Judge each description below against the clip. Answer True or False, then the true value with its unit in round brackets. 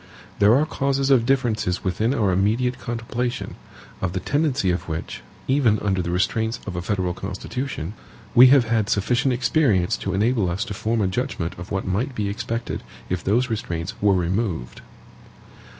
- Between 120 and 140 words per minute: False (165 wpm)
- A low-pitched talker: True (110 Hz)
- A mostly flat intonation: False (4.9 semitones)